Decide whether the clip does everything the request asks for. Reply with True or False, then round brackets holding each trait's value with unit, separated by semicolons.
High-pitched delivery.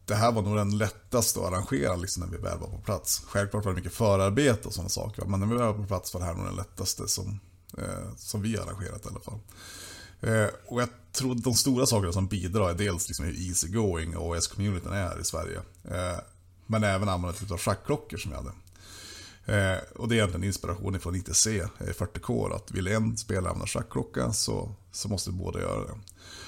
False (100 Hz)